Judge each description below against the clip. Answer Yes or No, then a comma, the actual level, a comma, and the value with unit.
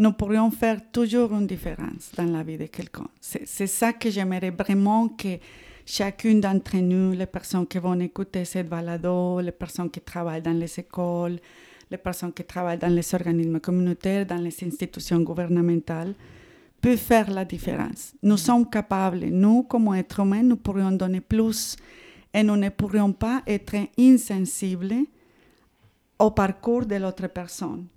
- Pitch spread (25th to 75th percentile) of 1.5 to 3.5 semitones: Yes, average, 3.2 semitones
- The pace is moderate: Yes, average, 160 wpm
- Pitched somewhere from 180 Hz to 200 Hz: Yes, high, 190 Hz